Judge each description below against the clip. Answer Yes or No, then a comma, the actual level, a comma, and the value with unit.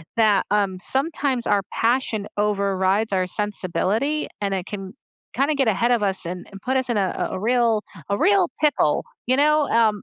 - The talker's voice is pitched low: No, high, 215 Hz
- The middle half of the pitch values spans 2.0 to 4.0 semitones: No, average, 4.9 semitones